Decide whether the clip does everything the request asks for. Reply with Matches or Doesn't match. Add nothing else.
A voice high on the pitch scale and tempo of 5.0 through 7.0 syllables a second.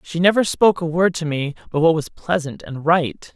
Doesn't match